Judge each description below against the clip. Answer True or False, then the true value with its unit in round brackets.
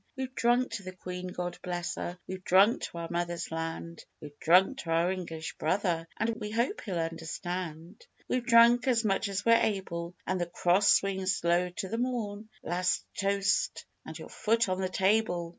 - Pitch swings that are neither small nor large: True (3.9 semitones)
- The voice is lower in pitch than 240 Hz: True (185 Hz)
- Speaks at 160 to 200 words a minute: True (185 wpm)